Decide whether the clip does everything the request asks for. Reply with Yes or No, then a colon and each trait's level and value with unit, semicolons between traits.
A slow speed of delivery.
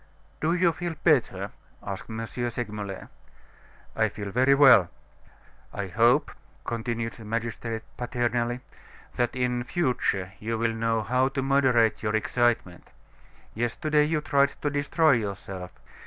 Yes: slow, 125 wpm